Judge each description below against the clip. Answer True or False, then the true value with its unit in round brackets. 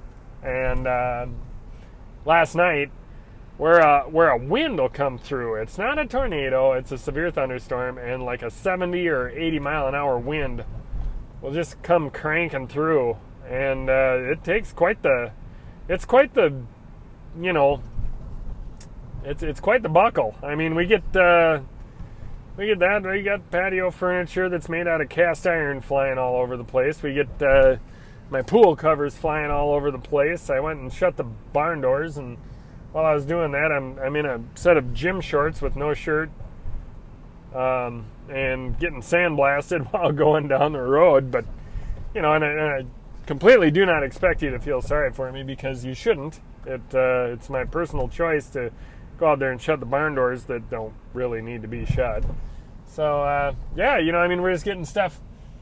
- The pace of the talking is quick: False (185 wpm)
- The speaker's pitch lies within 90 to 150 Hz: True (140 Hz)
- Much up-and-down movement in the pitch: False (4.3 semitones)